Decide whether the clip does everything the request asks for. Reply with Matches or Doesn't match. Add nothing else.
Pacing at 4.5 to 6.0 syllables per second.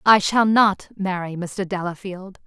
Doesn't match